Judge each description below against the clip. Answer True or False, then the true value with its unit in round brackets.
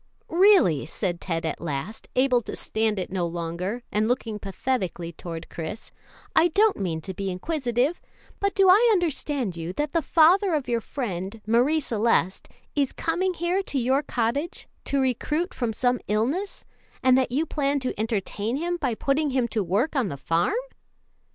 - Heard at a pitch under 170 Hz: False (245 Hz)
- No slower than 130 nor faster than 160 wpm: False (170 wpm)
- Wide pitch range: True (7.8 semitones)